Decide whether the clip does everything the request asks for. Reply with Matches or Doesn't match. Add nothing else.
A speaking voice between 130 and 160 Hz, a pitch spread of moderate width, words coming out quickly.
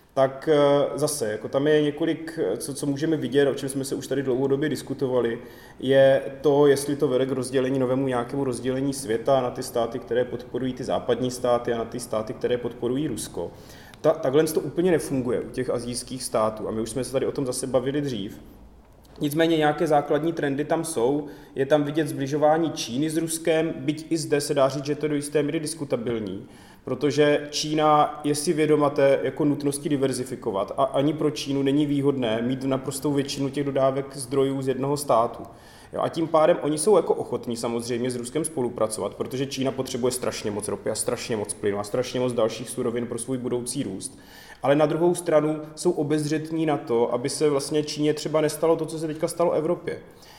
Matches